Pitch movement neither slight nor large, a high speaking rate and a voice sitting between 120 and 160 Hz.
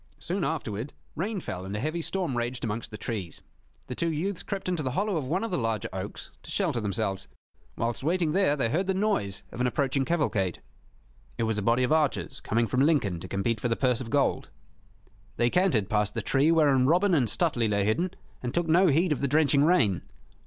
No: wide, 6.9 semitones; fast, 215 wpm; low, 135 Hz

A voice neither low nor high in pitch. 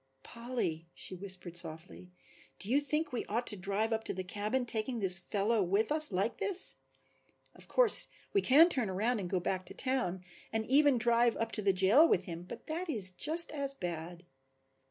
No: high, 220 Hz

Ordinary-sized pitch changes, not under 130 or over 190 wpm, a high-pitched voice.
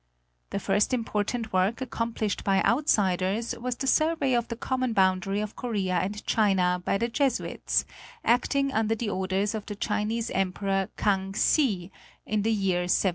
Yes: average, 3.4 semitones; average, 165 wpm; high, 210 Hz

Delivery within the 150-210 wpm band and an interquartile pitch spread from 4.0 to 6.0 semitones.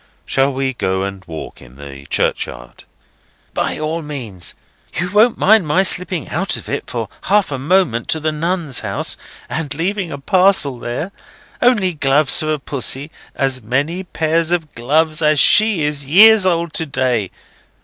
Yes: average, 160 wpm; average, 5.2 semitones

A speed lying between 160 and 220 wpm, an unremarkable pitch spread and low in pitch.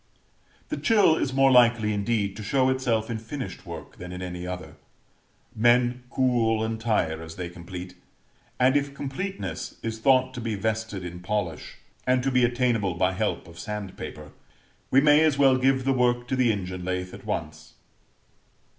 No: average, 175 wpm; wide, 5.8 semitones; low, 115 Hz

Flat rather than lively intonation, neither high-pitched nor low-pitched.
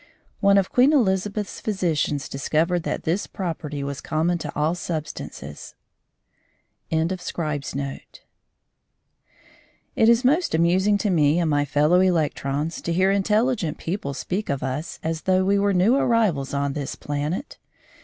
No: average, 5.1 semitones; medium, 170 Hz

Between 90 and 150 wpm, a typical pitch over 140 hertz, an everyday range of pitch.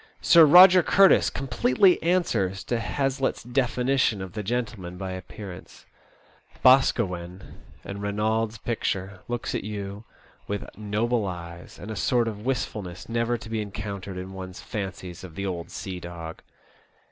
No: average, 145 wpm; low, 105 Hz; average, 4.4 semitones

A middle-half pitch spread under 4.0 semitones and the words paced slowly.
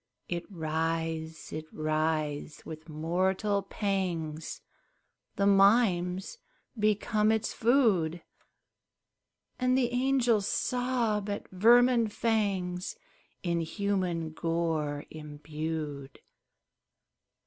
No: average, 5.1 semitones; slow, 80 wpm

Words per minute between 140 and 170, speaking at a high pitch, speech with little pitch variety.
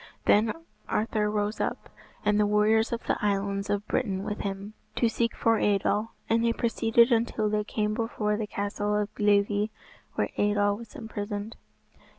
Yes: average, 165 wpm; high, 210 Hz; narrow, 1.6 semitones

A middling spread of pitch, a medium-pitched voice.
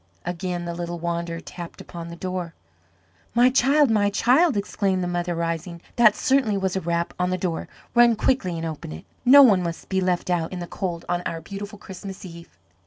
Yes: average, 3.2 semitones; medium, 180 Hz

